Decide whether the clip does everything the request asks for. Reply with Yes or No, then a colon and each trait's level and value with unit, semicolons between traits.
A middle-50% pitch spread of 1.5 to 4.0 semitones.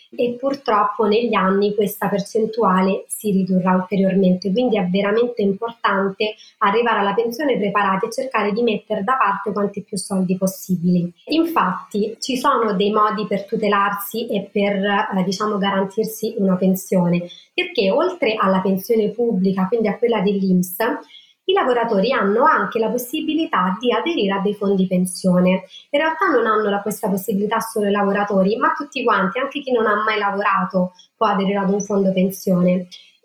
Yes: average, 2.8 semitones